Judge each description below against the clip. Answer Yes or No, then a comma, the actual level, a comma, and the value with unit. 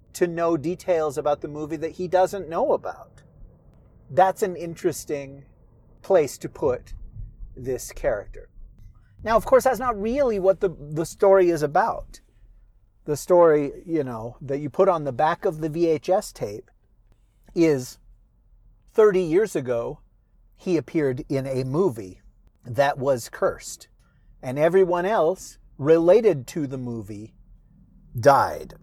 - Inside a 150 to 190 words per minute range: No, slow, 135 wpm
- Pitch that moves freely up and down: Yes, wide, 7.0 semitones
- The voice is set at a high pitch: No, medium, 150 Hz